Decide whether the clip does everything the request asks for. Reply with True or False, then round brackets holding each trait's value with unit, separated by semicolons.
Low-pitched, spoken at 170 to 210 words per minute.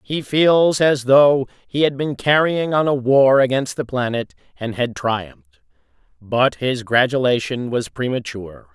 False (130 Hz; 150 wpm)